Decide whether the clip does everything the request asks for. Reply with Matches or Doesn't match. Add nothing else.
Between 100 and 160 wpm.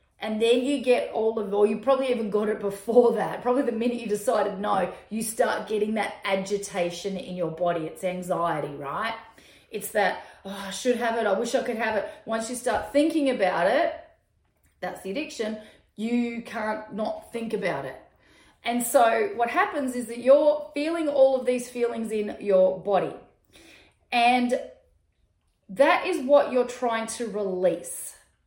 Doesn't match